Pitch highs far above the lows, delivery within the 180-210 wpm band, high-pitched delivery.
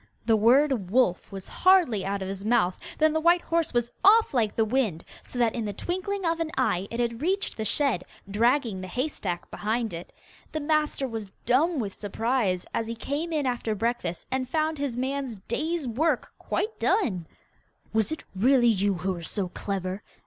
Yes: wide, 6.8 semitones; average, 190 wpm; high, 240 Hz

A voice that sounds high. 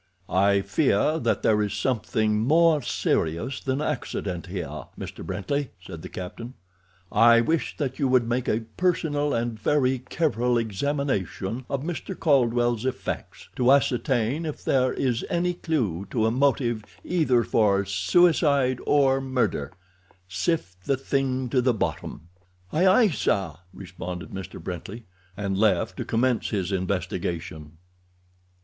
No: low, 120 Hz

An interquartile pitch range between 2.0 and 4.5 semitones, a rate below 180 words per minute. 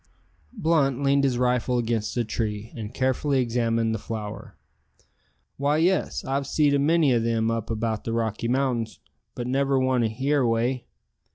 Yes: average, 3.2 semitones; average, 160 wpm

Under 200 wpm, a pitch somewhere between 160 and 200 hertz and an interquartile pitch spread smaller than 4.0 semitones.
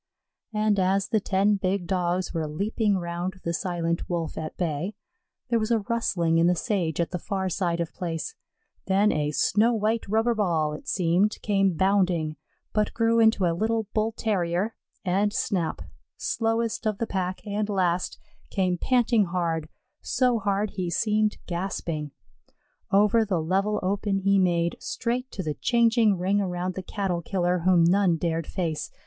Yes: average, 165 wpm; high, 190 Hz; average, 3.6 semitones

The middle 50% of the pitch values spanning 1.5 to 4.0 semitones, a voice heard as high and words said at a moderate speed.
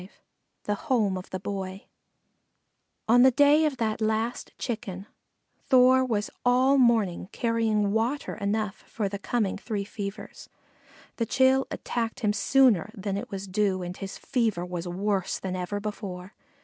Yes: average, 3.7 semitones; high, 210 Hz; average, 150 wpm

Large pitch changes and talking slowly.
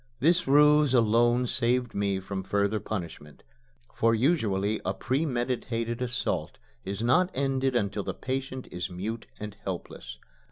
No: average, 4.5 semitones; slow, 130 wpm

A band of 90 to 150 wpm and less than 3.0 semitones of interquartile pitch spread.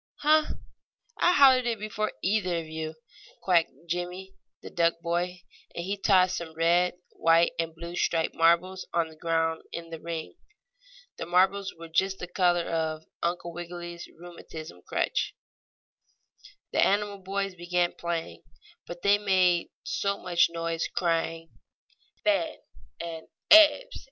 Yes: slow, 135 wpm; narrow, 2.5 semitones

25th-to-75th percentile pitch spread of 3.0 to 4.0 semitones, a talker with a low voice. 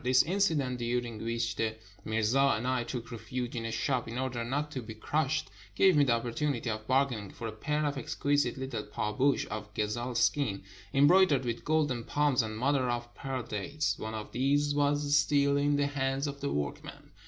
Yes: average, 3.7 semitones; low, 130 Hz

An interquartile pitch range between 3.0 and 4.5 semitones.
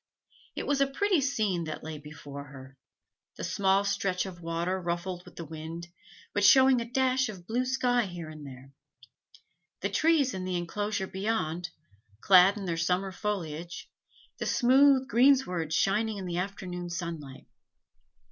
No: average, 5.0 semitones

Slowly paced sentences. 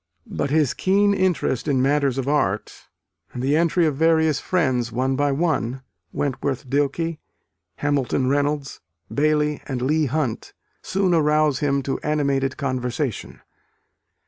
Yes: slow, 130 wpm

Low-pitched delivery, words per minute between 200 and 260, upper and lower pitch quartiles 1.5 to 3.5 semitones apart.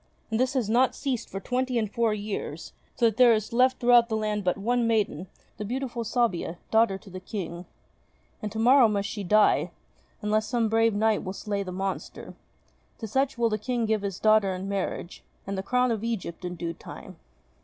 No: high, 215 Hz; fast, 205 wpm; average, 3.2 semitones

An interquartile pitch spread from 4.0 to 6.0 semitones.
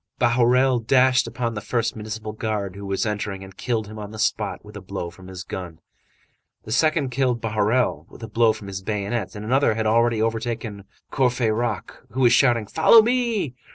No: average, 3.0 semitones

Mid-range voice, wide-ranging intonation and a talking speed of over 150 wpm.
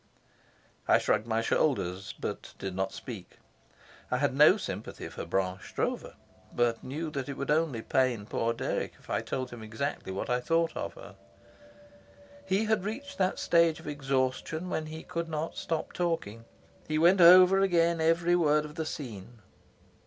Yes: medium, 150 Hz; wide, 6.2 semitones; average, 165 wpm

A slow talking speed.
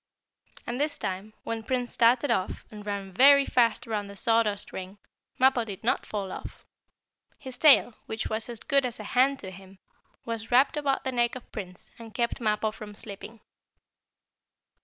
No: average, 175 wpm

